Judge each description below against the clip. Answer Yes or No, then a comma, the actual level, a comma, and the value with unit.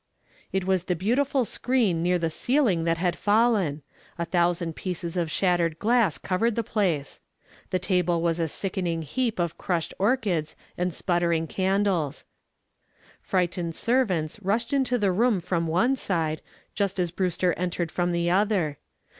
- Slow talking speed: No, average, 150 wpm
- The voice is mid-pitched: Yes, medium, 180 Hz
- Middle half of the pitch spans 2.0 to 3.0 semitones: No, average, 3.5 semitones